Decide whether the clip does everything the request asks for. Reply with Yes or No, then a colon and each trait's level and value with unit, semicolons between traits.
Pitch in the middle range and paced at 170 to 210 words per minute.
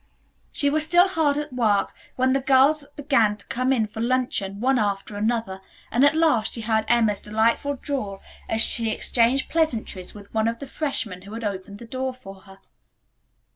No: high, 235 Hz; average, 185 wpm